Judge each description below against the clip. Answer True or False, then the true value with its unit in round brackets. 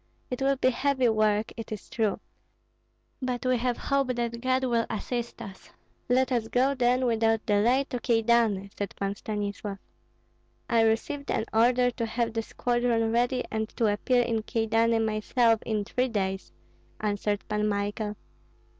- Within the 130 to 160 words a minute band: True (155 wpm)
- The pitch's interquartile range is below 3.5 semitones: True (2.5 semitones)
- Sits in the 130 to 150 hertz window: False (230 Hz)